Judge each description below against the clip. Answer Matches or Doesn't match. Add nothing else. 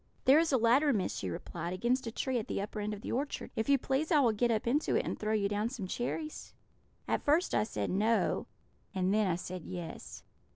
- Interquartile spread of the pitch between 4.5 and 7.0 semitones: Matches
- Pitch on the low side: Doesn't match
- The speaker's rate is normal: Doesn't match